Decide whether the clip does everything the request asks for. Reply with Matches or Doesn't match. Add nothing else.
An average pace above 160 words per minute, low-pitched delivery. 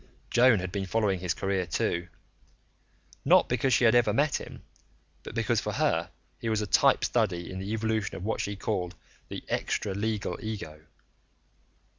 Matches